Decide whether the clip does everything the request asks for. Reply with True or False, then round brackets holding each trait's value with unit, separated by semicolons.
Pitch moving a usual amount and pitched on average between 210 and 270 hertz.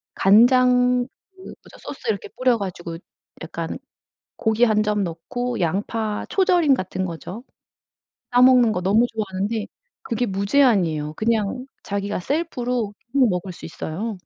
True (4.6 semitones; 220 Hz)